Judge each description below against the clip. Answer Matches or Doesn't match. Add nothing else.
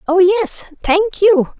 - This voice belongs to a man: Doesn't match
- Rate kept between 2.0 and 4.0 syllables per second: Matches